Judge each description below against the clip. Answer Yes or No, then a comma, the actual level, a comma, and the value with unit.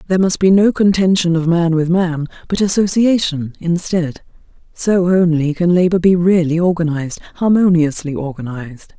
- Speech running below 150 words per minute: Yes, average, 140 wpm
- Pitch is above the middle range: No, medium, 170 Hz